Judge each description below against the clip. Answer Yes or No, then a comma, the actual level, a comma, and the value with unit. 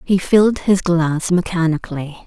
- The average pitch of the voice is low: No, medium, 175 Hz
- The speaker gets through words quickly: No, slow, 135 wpm